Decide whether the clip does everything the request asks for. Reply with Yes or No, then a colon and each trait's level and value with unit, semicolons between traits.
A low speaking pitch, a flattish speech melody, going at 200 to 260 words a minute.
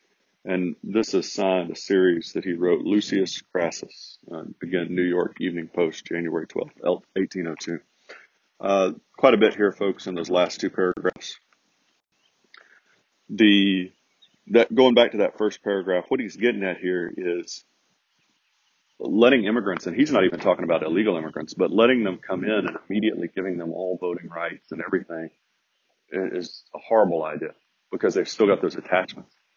No: very low, 95 Hz; narrow, 2.2 semitones; average, 160 wpm